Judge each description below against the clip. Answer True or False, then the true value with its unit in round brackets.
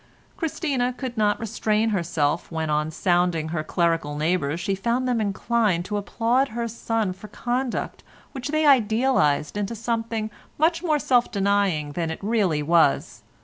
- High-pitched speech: True (210 Hz)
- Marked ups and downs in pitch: True (5.9 semitones)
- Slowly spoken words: False (150 wpm)